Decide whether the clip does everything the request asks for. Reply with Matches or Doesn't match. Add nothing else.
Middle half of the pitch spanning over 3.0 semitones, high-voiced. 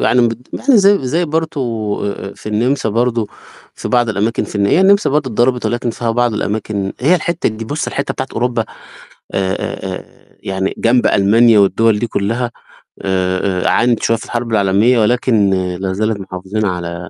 Doesn't match